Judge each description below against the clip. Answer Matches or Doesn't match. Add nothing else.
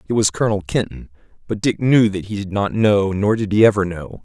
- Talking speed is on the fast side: Matches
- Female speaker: Doesn't match